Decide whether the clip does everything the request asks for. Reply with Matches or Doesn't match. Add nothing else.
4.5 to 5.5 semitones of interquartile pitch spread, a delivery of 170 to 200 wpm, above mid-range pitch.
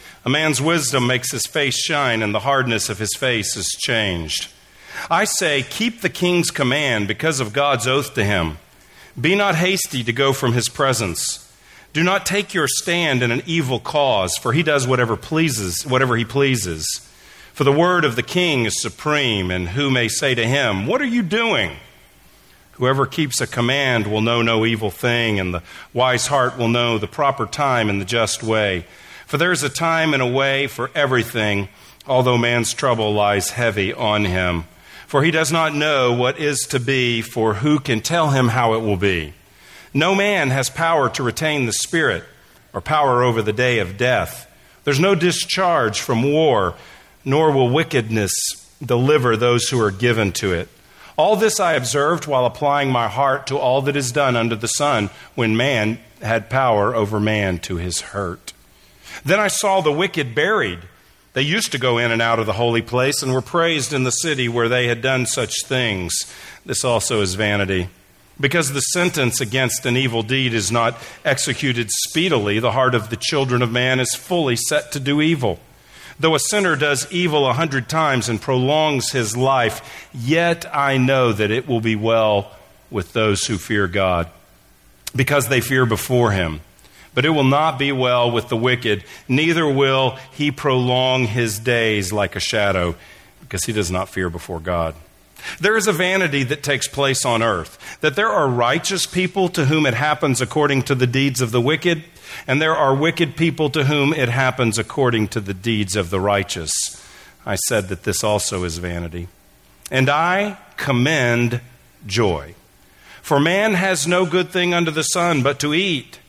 Doesn't match